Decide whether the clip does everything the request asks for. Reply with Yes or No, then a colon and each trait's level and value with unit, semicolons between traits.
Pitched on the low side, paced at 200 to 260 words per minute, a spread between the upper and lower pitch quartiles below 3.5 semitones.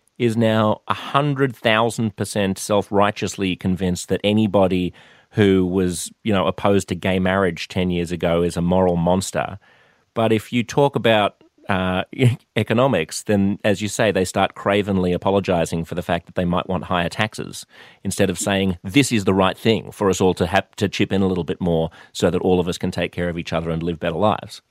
Yes: very low, 95 Hz; fast, 205 wpm; average, 2.7 semitones